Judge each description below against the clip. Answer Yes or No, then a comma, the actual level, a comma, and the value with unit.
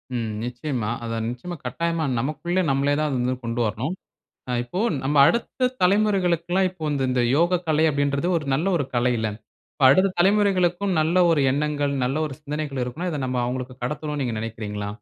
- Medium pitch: Yes, medium, 145 Hz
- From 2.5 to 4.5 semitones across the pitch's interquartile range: No, wide, 5.6 semitones